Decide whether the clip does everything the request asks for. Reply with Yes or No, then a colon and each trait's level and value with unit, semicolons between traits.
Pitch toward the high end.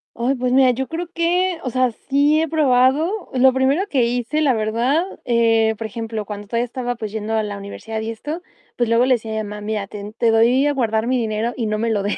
Yes: high, 240 Hz